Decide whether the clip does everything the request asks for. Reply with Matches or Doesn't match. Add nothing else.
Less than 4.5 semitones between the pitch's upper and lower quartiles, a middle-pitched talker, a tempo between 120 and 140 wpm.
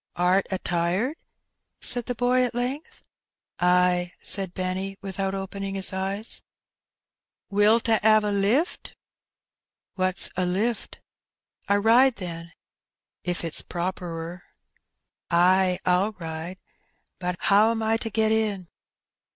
Doesn't match